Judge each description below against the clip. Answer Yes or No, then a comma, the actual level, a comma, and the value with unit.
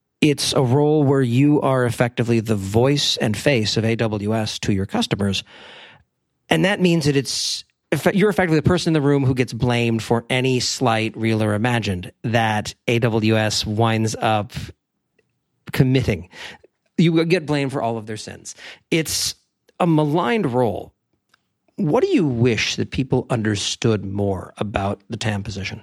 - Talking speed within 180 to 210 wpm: No, average, 155 wpm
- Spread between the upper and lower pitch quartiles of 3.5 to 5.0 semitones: Yes, average, 4.5 semitones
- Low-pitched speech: Yes, low, 120 Hz